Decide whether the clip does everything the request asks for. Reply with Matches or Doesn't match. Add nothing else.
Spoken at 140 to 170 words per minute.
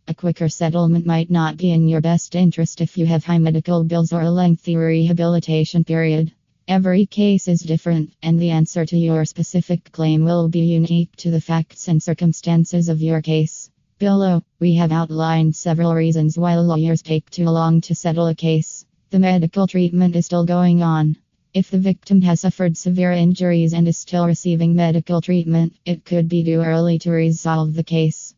Doesn't match